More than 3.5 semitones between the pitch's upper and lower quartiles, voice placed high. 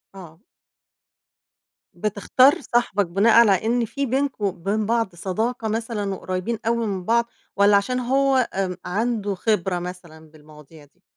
Yes: average, 4.2 semitones; high, 205 Hz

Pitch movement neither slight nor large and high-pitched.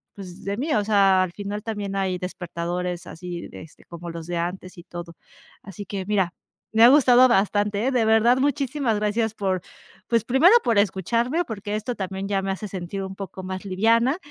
Yes: average, 3.6 semitones; high, 200 Hz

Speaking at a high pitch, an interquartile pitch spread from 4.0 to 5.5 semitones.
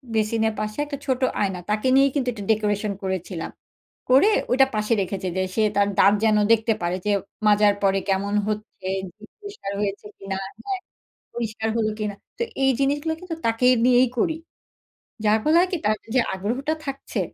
Yes: high, 215 Hz; average, 4.7 semitones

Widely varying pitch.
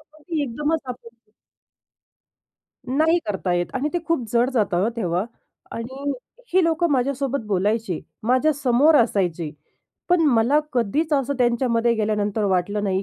Yes: wide, 5.8 semitones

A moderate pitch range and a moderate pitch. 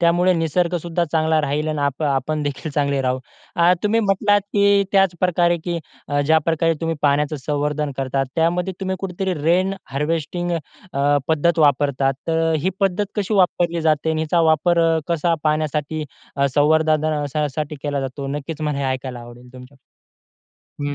Yes: average, 3.2 semitones; medium, 155 Hz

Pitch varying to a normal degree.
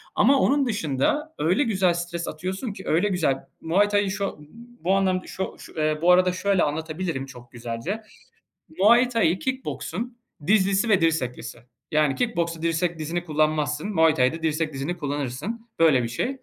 Yes: average, 4.7 semitones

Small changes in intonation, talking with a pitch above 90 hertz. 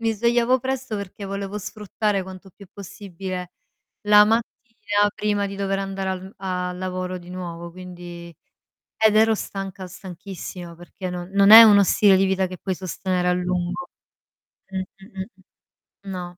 Yes: narrow, 2.2 semitones; high, 190 Hz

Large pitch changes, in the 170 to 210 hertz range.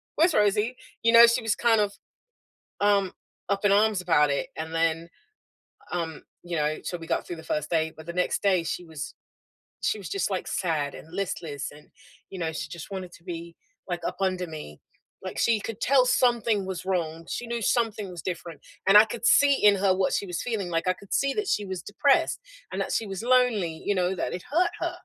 No: average, 4.5 semitones; high, 190 Hz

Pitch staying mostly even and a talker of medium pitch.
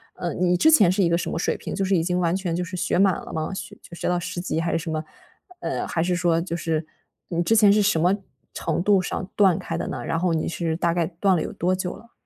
Yes: narrow, 2.2 semitones; medium, 175 Hz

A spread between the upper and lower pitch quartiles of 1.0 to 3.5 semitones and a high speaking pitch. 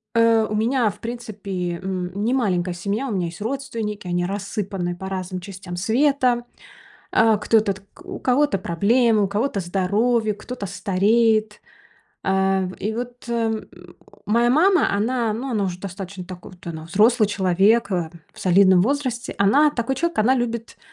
No: average, 3.9 semitones; high, 210 Hz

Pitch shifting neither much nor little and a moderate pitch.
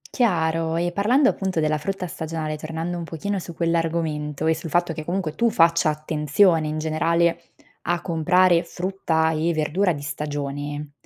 No: narrow, 2.2 semitones; medium, 165 Hz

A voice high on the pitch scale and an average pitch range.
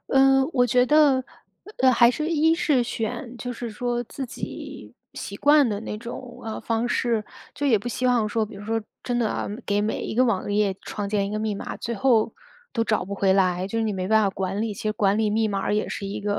Yes: high, 225 Hz; average, 3.2 semitones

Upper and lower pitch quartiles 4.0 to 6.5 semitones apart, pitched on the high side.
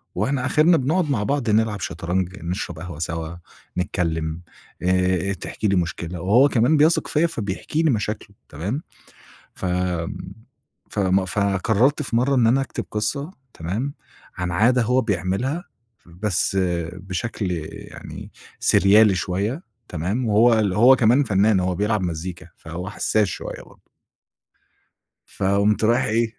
No: average, 5.1 semitones; low, 105 Hz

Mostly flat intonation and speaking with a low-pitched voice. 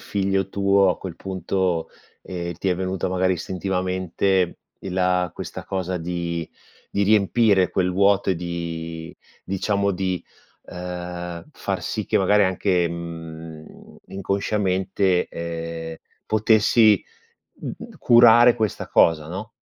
Yes: narrow, 2.3 semitones; very low, 95 Hz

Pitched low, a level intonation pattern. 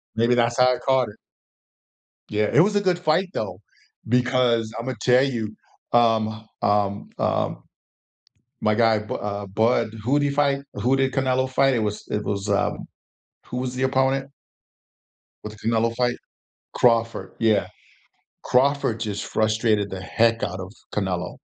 No: low, 115 Hz; average, 3.5 semitones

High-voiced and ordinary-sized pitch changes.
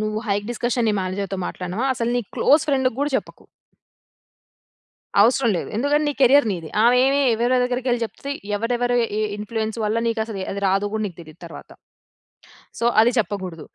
Yes: high, 230 Hz; average, 3.7 semitones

